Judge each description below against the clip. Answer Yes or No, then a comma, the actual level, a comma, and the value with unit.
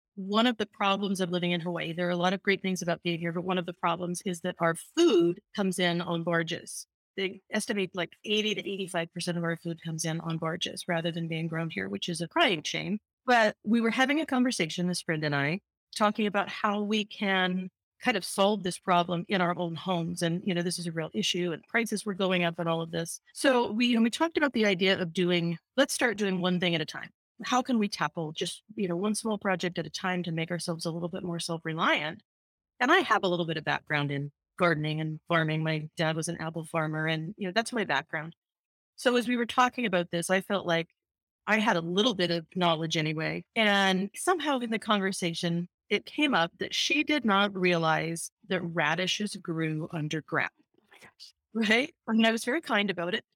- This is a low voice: No, medium, 180 Hz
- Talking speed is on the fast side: Yes, fast, 230 wpm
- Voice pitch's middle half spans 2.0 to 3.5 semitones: No, average, 4.0 semitones